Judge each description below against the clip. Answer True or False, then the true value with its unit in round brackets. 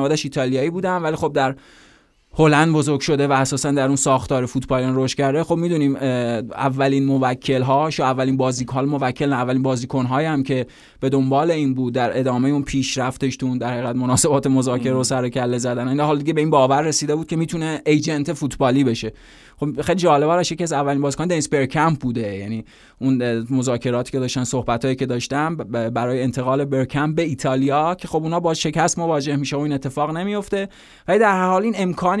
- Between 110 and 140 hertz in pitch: True (135 Hz)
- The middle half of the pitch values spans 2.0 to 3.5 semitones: True (3.1 semitones)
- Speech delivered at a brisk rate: True (190 wpm)